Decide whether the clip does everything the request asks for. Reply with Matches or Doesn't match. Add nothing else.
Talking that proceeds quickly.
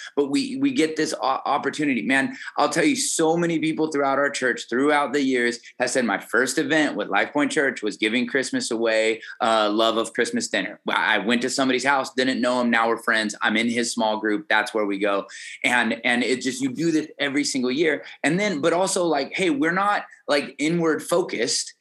Matches